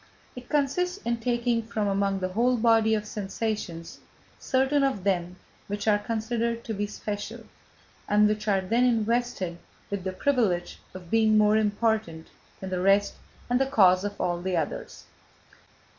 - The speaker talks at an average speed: Yes, average, 160 wpm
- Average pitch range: Yes, average, 3.4 semitones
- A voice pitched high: Yes, high, 215 Hz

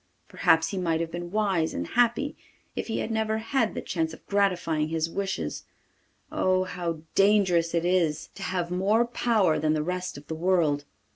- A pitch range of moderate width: Yes, average, 3.8 semitones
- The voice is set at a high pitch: No, medium, 180 Hz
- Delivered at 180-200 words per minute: Yes, average, 185 wpm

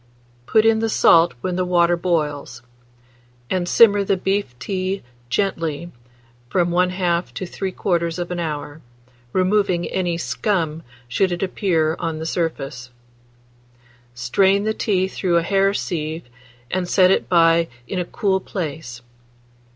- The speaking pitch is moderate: Yes, medium, 175 Hz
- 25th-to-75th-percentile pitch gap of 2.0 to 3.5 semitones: Yes, narrow, 2.6 semitones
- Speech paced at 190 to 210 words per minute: No, slow, 135 wpm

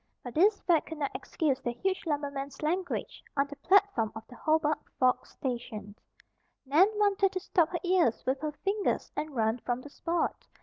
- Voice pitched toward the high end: Yes, very high, 300 Hz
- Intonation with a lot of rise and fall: Yes, wide, 6.1 semitones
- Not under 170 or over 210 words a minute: Yes, average, 180 wpm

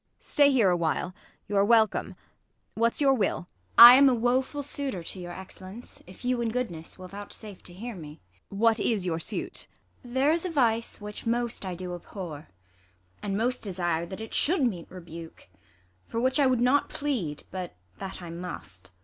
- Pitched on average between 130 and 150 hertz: No, high, 210 Hz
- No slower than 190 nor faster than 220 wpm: Yes, average, 195 wpm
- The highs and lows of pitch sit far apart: Yes, wide, 5.7 semitones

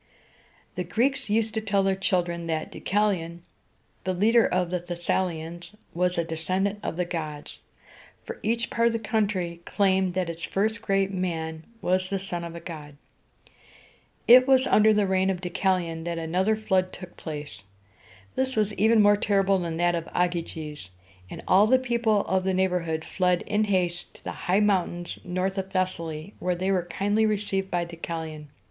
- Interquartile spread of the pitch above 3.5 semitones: No, average, 3.2 semitones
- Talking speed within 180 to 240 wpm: Yes, average, 185 wpm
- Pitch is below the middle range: No, medium, 185 Hz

